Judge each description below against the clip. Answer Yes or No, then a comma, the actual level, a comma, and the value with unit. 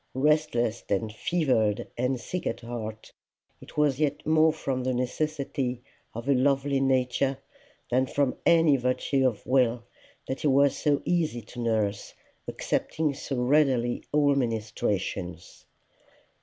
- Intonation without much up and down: No, average, 3.2 semitones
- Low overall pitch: Yes, low, 130 Hz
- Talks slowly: Yes, slow, 130 wpm